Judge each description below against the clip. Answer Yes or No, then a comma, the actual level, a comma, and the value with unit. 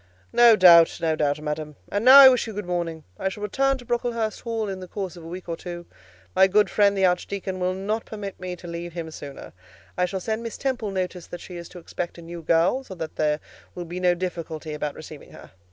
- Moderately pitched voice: Yes, medium, 180 Hz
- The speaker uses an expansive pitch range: No, average, 3.7 semitones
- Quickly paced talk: Yes, fast, 240 wpm